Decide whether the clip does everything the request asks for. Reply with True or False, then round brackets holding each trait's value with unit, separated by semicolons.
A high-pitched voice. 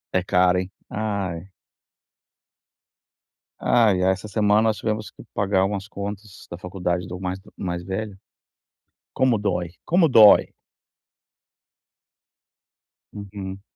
False (100 Hz)